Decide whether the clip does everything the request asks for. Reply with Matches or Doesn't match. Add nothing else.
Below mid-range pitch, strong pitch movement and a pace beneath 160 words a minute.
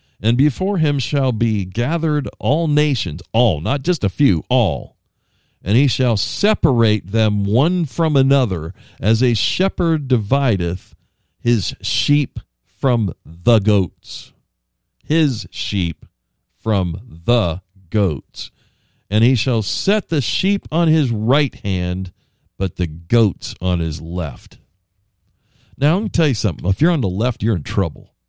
Matches